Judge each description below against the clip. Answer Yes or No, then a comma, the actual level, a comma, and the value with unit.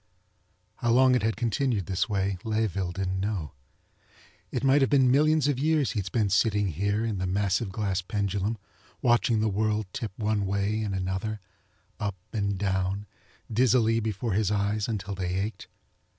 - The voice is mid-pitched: No, low, 105 Hz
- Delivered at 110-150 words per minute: No, average, 165 wpm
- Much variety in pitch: No, average, 2.9 semitones